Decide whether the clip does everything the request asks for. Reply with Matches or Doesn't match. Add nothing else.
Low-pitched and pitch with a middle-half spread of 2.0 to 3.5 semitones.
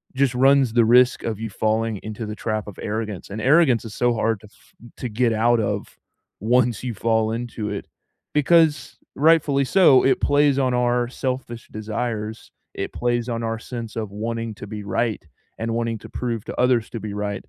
Matches